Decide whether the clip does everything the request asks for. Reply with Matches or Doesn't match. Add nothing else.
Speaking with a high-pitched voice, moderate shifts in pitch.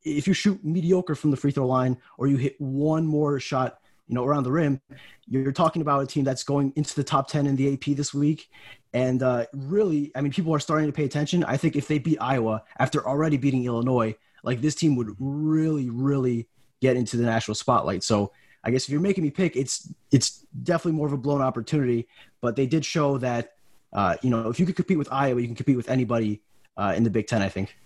Doesn't match